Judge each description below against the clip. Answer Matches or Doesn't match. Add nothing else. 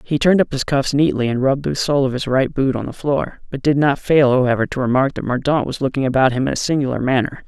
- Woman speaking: Doesn't match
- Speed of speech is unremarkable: Doesn't match